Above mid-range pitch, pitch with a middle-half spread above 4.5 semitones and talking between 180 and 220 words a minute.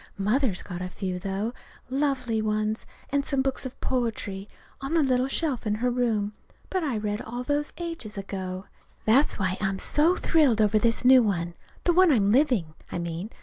Yes: high, 225 Hz; wide, 5.4 semitones; average, 185 wpm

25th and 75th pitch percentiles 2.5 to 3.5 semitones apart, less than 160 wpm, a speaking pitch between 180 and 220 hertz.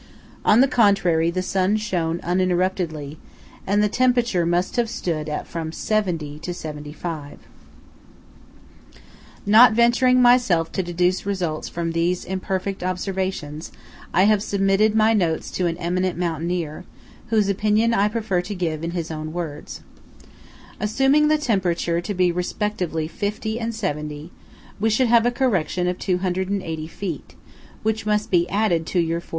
No: average, 4.1 semitones; average, 145 wpm; medium, 185 Hz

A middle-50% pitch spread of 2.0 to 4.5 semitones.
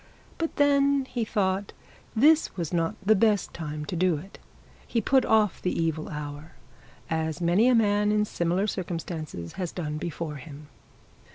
No: average, 5.2 semitones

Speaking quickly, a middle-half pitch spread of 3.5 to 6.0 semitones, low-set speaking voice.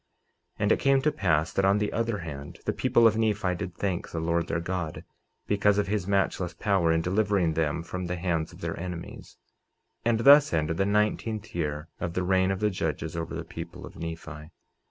Yes: fast, 215 wpm; average, 3.8 semitones; very low, 90 Hz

